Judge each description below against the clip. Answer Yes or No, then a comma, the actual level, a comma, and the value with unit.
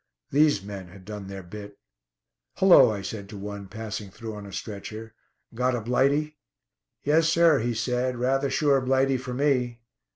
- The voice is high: No, low, 120 Hz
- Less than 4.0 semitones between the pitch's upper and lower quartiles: No, average, 4.8 semitones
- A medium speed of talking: Yes, average, 165 wpm